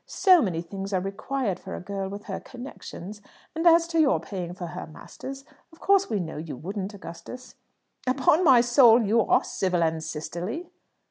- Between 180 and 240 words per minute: Yes, average, 185 wpm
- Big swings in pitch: Yes, wide, 6.9 semitones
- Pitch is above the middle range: Yes, high, 205 Hz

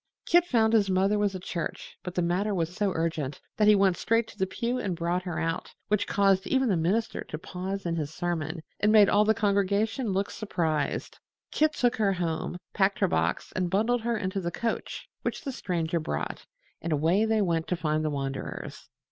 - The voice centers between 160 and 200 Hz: Yes, high, 190 Hz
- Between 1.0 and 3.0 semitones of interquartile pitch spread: No, average, 4.1 semitones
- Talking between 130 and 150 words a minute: No, fast, 205 wpm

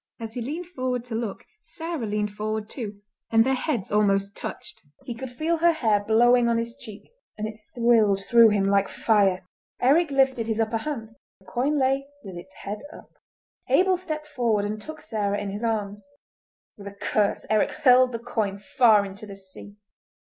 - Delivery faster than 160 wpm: Yes, average, 185 wpm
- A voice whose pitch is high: Yes, high, 225 Hz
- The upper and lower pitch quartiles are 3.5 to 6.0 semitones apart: Yes, average, 3.9 semitones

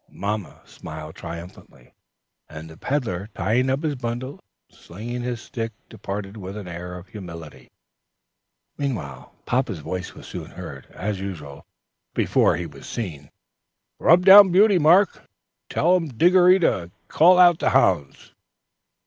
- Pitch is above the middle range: No, low, 110 Hz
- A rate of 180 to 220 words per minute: No, slow, 135 wpm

